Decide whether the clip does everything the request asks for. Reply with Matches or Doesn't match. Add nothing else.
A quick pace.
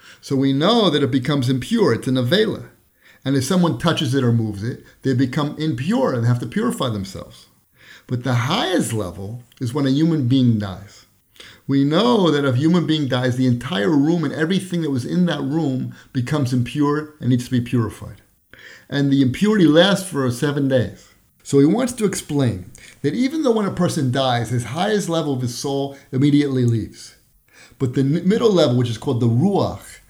Doesn't match